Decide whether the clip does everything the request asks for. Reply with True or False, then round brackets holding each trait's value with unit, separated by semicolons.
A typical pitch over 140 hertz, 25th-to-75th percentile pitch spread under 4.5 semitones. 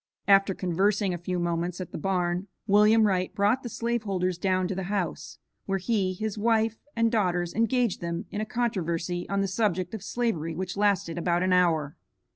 True (190 Hz; 3.2 semitones)